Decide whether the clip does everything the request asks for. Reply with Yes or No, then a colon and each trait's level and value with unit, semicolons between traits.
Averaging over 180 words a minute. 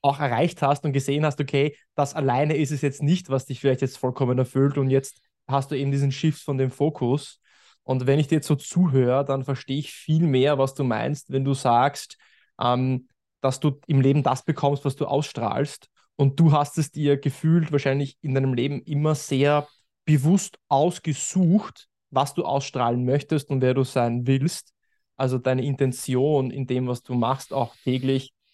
Yes: fast, 190 wpm